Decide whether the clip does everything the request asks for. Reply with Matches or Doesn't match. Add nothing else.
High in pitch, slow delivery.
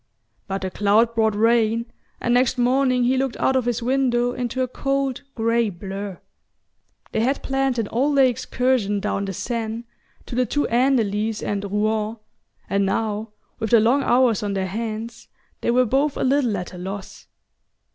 Doesn't match